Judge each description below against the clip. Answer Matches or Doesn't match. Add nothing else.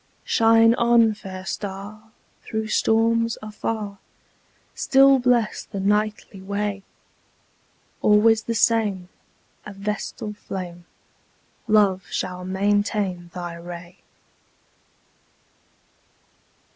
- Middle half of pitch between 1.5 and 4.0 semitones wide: Matches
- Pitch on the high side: Matches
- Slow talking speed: Matches